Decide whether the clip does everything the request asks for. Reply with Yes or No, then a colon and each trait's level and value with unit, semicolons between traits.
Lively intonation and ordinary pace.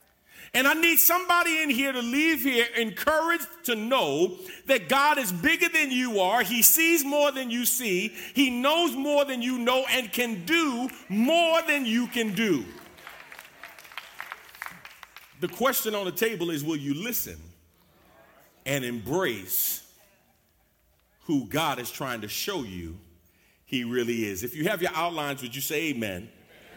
Yes: wide, 9.0 semitones; average, 155 wpm